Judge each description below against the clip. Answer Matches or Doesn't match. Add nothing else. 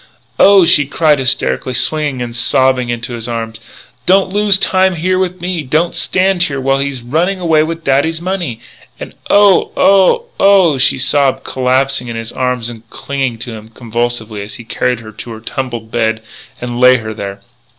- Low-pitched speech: Matches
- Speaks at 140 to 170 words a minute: Doesn't match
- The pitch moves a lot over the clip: Matches